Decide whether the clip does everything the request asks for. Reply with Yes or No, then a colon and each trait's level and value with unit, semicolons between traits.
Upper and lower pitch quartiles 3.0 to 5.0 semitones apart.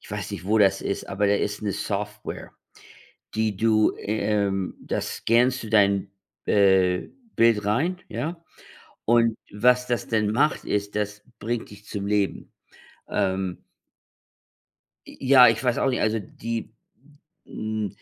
No: narrow, 2.4 semitones